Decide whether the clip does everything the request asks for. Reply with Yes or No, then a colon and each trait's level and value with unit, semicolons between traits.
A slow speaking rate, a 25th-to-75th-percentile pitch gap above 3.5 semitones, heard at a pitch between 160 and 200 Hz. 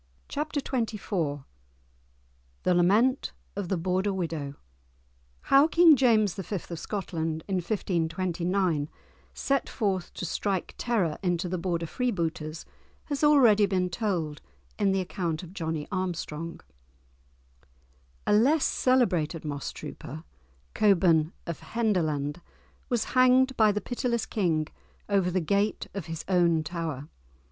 Yes: slow, 120 wpm; average, 4.7 semitones; medium, 185 Hz